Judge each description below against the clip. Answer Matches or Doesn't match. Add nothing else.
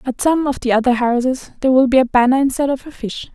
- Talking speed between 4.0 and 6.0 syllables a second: Doesn't match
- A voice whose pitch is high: Matches